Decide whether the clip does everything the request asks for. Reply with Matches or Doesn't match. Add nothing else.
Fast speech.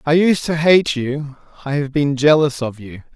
Matches